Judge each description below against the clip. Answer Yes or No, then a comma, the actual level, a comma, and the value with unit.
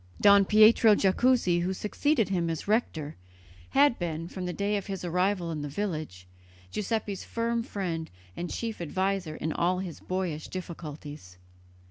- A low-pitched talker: No, medium, 185 Hz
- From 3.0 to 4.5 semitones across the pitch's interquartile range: Yes, average, 4.1 semitones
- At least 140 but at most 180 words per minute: Yes, average, 150 wpm